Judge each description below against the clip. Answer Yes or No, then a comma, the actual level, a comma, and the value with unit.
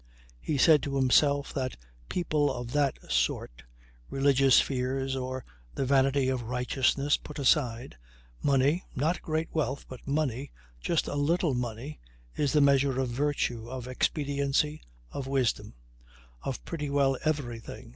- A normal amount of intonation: No, narrow, 2.3 semitones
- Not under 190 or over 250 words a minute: No, average, 140 wpm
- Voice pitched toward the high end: No, low, 135 Hz